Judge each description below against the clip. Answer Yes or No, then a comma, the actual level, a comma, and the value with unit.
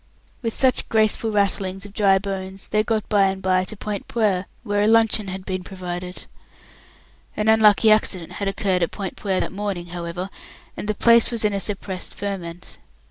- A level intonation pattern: Yes, narrow, 2.3 semitones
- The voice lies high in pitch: Yes, high, 200 Hz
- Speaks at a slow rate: No, average, 185 wpm